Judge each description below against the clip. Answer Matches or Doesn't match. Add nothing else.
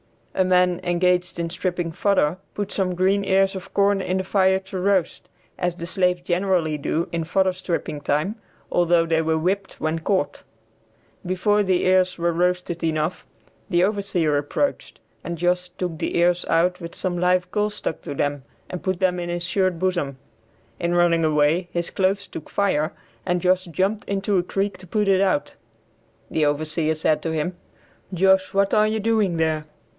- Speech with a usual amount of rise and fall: Doesn't match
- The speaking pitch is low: Doesn't match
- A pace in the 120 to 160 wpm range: Doesn't match